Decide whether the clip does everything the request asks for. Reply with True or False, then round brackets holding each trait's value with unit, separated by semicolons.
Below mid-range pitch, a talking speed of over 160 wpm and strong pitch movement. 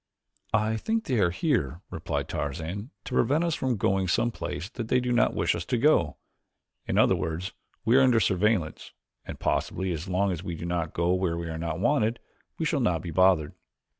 True (95 Hz; 200 wpm; 6.0 semitones)